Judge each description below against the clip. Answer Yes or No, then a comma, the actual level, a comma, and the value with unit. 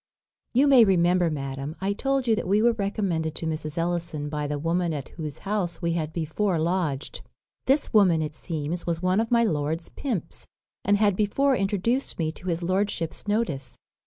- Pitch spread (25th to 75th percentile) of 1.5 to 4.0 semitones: No, average, 4.7 semitones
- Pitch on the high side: No, medium, 175 Hz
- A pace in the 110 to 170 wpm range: No, average, 185 wpm